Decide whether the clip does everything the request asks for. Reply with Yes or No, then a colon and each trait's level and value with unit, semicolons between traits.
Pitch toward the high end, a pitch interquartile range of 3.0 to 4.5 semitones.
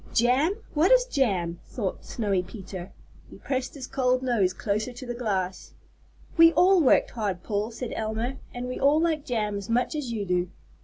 No: high, 240 Hz; average, 5.0 semitones